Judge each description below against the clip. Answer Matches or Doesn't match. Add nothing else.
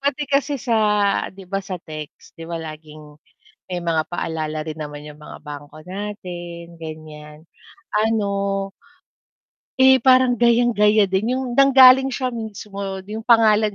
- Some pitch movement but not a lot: Doesn't match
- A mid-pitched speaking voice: Doesn't match